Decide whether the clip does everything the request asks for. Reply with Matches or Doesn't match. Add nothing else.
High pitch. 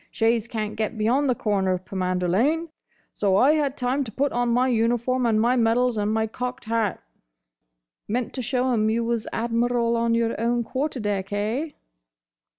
Matches